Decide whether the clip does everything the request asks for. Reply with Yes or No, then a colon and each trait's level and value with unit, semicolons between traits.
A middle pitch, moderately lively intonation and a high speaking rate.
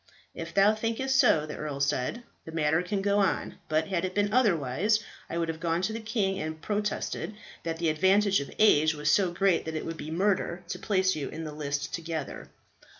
Yes: medium, 175 Hz; average, 4.5 semitones; fast, 210 wpm